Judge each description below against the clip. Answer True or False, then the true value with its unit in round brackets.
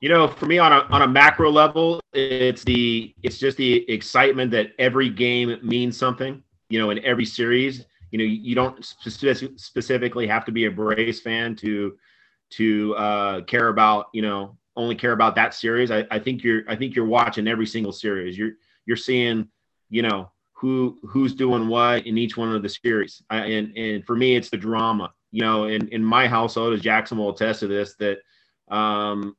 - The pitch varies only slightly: True (2.3 semitones)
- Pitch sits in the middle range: False (115 Hz)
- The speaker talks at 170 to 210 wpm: True (200 wpm)